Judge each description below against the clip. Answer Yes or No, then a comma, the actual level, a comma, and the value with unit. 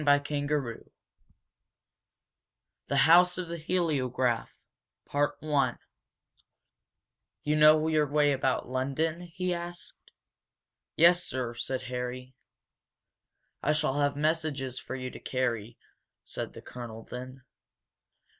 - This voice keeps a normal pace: No, slow, 100 wpm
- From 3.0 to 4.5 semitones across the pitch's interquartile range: Yes, average, 3.7 semitones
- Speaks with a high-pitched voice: No, medium, 145 Hz